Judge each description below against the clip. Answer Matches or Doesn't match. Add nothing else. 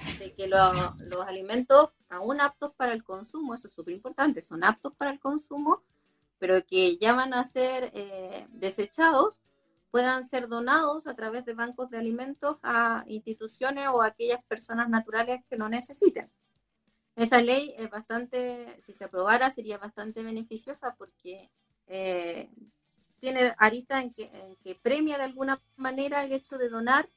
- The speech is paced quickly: Doesn't match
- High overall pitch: Matches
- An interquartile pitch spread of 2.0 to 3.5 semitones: Doesn't match